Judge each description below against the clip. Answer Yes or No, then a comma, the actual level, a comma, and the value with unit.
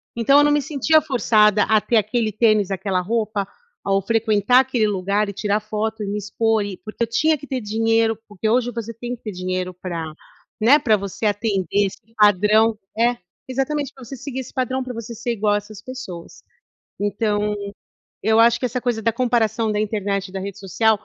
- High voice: Yes, high, 220 Hz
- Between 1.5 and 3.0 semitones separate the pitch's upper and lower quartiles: Yes, average, 2.7 semitones